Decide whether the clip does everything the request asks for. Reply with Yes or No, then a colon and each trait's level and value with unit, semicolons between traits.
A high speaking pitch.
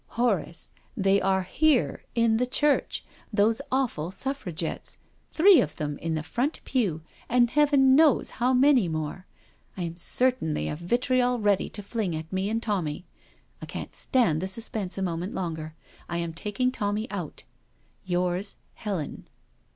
Yes: high, 200 Hz